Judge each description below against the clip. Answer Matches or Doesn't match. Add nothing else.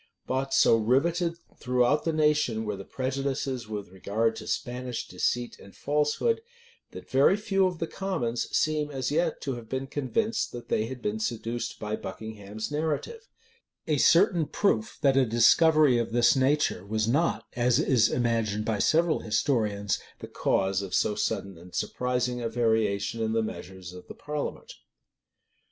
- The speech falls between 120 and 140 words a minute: Doesn't match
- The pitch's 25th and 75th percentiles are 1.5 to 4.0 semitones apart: Doesn't match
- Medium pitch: Doesn't match